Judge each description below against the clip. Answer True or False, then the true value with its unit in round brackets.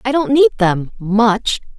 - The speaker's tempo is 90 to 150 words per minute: True (135 wpm)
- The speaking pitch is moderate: False (230 Hz)